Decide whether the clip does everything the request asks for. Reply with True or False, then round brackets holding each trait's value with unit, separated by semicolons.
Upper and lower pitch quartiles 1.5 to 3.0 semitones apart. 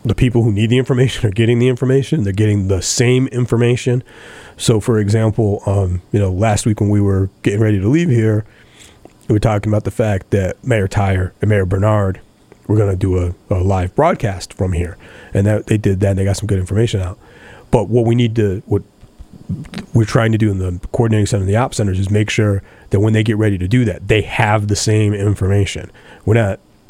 True (2.7 semitones)